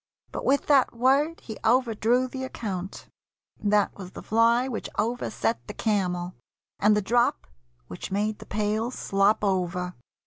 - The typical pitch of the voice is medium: No, high, 215 Hz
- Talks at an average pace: Yes, average, 145 wpm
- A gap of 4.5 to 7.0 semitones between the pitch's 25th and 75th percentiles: No, average, 3.6 semitones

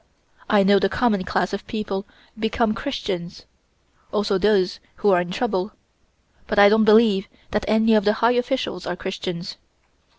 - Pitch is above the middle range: Yes, high, 205 Hz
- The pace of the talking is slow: No, average, 160 wpm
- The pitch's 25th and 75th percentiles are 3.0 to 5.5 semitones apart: No, narrow, 2.4 semitones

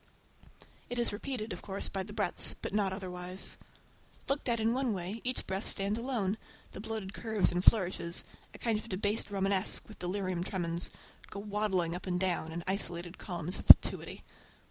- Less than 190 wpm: Yes, average, 165 wpm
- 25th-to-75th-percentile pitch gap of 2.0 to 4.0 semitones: Yes, average, 3.2 semitones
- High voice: Yes, high, 195 Hz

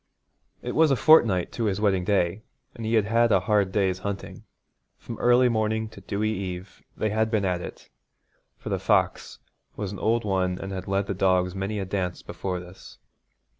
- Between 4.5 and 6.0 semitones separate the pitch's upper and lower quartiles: No, average, 2.8 semitones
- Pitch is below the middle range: Yes, low, 100 Hz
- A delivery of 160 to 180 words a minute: No, average, 195 wpm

